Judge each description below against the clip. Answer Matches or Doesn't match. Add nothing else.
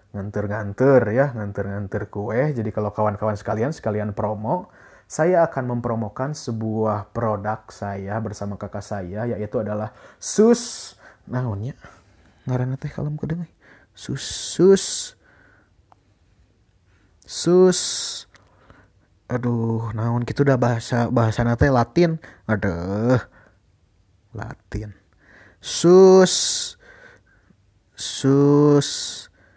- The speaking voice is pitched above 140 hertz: Doesn't match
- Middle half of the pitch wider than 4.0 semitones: Matches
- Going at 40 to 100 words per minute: Matches